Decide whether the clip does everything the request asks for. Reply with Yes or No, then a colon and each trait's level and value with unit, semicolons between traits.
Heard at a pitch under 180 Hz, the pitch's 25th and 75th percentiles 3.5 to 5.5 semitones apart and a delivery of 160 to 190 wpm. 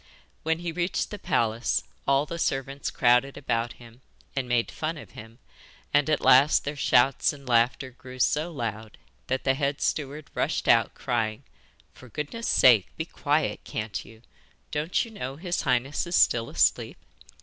Yes: low, 135 Hz; average, 4.1 semitones; average, 165 wpm